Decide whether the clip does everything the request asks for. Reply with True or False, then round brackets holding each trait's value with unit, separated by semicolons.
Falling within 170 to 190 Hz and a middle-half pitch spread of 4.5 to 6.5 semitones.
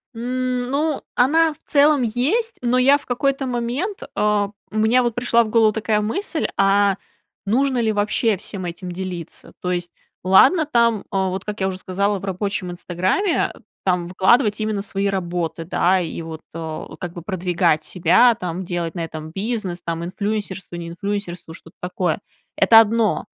False (200 Hz; 5.1 semitones)